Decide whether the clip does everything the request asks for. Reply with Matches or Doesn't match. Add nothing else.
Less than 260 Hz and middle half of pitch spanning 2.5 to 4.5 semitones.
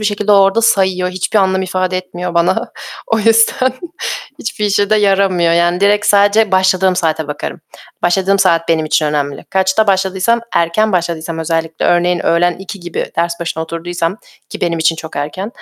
Matches